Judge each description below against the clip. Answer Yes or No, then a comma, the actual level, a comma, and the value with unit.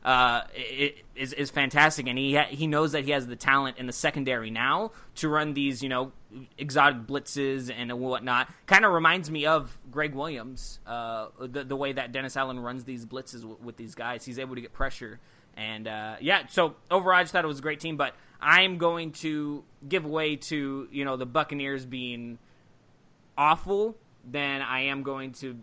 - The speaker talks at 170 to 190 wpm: No, average, 200 wpm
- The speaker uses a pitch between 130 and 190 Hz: Yes, low, 135 Hz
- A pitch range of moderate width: Yes, average, 3.2 semitones